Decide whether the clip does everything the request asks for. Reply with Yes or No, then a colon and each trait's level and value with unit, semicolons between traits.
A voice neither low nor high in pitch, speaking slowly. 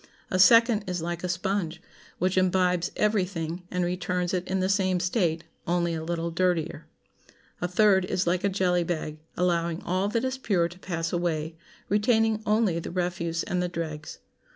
No: medium, 180 Hz; average, 175 wpm